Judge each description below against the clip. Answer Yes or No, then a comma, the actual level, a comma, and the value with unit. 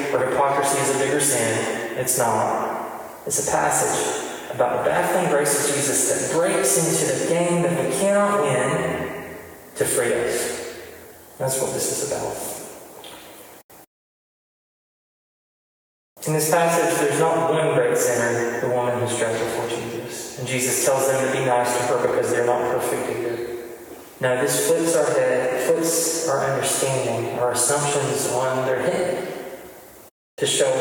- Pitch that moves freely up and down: Yes, wide, 6.7 semitones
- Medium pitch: Yes, medium, 145 Hz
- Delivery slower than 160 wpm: Yes, average, 140 wpm